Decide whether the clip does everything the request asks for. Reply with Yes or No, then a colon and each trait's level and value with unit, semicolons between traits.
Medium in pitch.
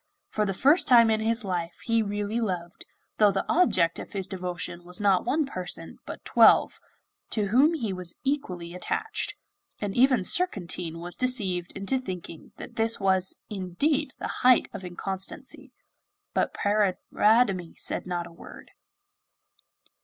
No: high, 195 Hz